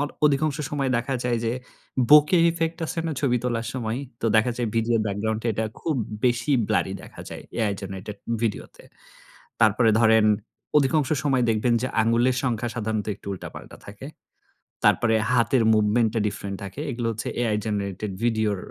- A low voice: Yes, low, 115 Hz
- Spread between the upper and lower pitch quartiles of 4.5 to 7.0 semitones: No, average, 2.9 semitones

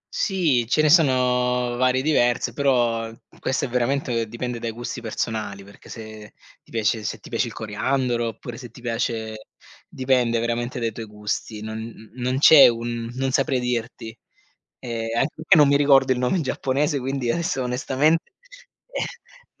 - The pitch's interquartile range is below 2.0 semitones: No, average, 2.8 semitones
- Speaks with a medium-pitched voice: No, low, 125 Hz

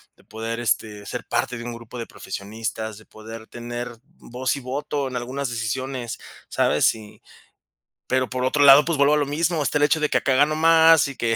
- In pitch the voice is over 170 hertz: No, low, 125 Hz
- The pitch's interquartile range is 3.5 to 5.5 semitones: Yes, average, 3.9 semitones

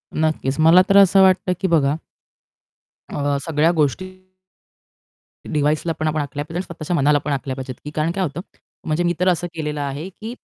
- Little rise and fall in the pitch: No, average, 3.3 semitones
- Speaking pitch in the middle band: Yes, medium, 155 Hz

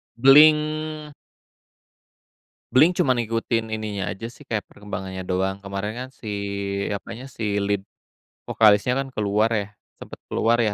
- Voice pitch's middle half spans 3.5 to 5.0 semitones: Yes, average, 4.3 semitones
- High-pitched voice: No, low, 110 Hz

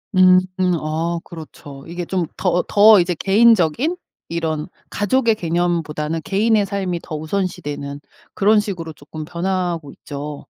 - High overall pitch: No, medium, 175 Hz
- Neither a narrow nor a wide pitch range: Yes, average, 3.8 semitones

